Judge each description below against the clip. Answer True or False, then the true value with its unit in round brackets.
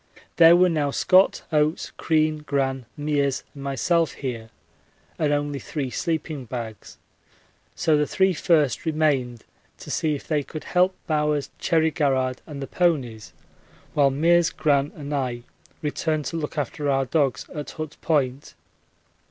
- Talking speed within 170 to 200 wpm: False (145 wpm)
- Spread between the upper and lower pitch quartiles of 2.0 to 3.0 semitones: True (2.6 semitones)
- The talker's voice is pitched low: False (150 Hz)